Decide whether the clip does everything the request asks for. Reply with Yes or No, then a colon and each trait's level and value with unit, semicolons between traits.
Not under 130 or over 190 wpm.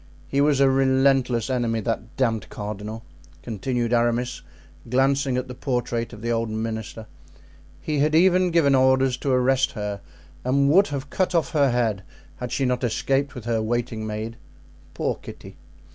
Yes: average, 160 wpm